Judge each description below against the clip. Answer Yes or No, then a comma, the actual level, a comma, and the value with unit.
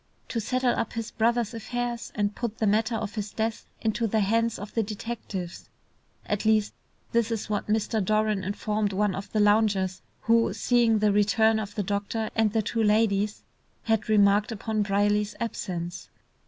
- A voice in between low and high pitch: No, high, 215 Hz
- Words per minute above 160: Yes, average, 170 wpm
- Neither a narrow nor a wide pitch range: No, narrow, 1.8 semitones